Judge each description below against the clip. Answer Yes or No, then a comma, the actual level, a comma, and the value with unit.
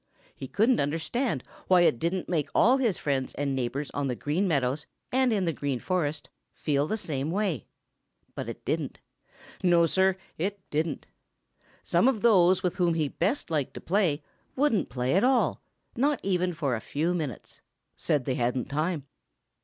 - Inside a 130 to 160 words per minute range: No, average, 170 wpm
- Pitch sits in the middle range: Yes, medium, 165 Hz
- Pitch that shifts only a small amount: No, average, 5.1 semitones